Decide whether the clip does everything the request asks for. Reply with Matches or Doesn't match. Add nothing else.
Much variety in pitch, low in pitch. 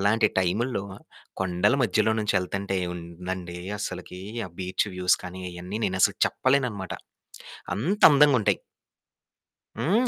Doesn't match